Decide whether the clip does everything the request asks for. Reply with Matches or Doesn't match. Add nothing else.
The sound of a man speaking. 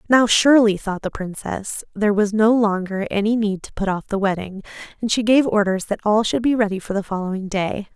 Doesn't match